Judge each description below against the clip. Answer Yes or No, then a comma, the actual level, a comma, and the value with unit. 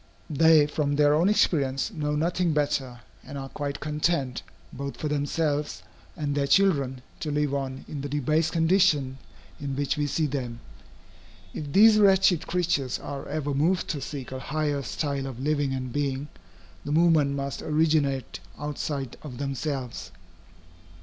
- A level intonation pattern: Yes, narrow, 2.2 semitones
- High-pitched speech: No, medium, 145 Hz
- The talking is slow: No, average, 150 wpm